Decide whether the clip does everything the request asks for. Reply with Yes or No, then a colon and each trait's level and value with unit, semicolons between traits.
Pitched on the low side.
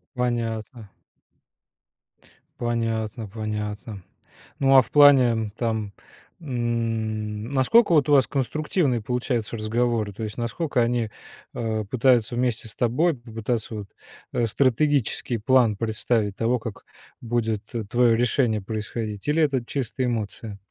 Yes: low, 115 Hz